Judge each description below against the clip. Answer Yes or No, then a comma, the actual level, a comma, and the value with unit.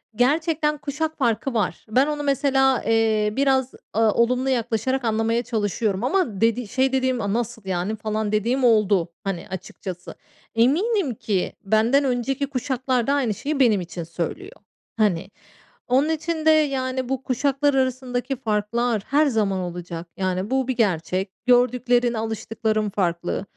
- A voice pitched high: Yes, high, 240 Hz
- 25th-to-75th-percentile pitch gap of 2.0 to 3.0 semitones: No, average, 4.0 semitones